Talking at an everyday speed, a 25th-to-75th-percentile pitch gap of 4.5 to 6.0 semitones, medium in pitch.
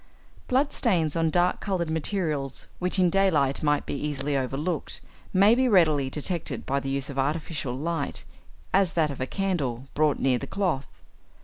Yes: average, 175 wpm; average, 4.8 semitones; medium, 155 Hz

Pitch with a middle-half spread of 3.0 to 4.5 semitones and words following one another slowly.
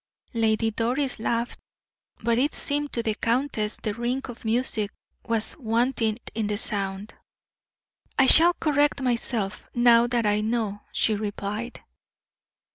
No: narrow, 2.4 semitones; slow, 130 wpm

